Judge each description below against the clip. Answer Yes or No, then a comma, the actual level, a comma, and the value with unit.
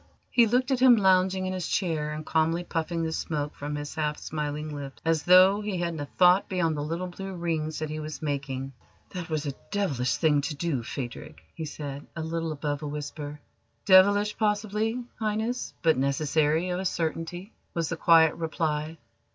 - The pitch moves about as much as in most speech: Yes, average, 3.8 semitones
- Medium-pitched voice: Yes, medium, 160 Hz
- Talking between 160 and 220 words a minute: Yes, average, 185 wpm